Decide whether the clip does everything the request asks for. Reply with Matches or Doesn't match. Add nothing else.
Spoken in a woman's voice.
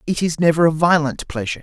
Doesn't match